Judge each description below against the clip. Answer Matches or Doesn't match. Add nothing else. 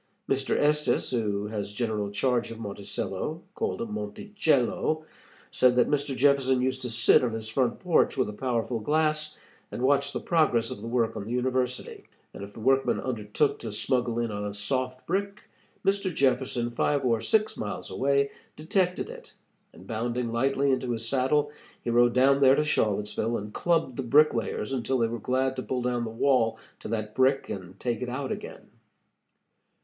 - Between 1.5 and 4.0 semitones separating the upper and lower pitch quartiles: Matches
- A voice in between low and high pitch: Doesn't match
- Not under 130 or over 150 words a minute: Doesn't match